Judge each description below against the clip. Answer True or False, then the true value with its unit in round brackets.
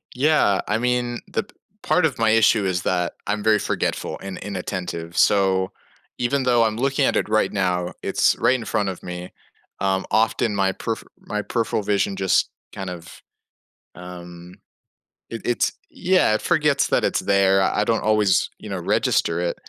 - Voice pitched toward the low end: True (105 Hz)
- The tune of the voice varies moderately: True (3.8 semitones)